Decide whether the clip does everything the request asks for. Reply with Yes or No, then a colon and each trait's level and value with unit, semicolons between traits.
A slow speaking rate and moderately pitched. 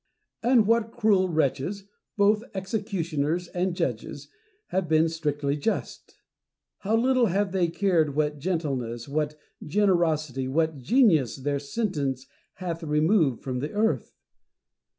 Yes: slow, 125 wpm; medium, 165 Hz